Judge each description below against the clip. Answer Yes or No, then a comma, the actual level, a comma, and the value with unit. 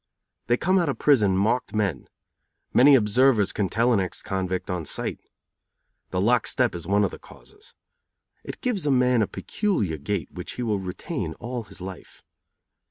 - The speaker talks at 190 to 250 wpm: No, average, 175 wpm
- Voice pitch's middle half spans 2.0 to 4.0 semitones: No, average, 5.1 semitones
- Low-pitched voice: Yes, low, 110 Hz